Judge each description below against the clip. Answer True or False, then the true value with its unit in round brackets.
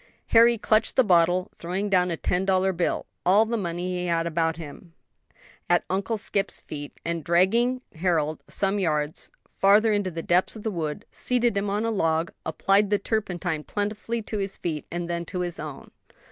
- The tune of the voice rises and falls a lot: False (3.5 semitones)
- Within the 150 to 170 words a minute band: False (190 wpm)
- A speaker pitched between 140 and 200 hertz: True (185 Hz)